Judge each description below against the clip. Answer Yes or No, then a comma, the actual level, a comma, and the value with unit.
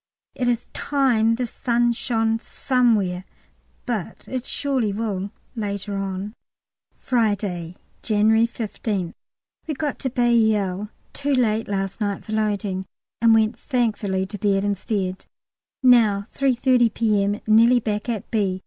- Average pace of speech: No, slow, 125 wpm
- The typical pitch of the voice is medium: No, high, 220 Hz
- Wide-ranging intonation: No, average, 3.1 semitones